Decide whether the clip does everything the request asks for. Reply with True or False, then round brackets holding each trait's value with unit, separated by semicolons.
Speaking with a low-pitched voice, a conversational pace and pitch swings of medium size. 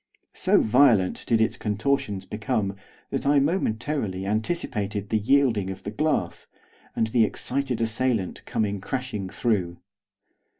False (110 Hz; 125 wpm; 4.2 semitones)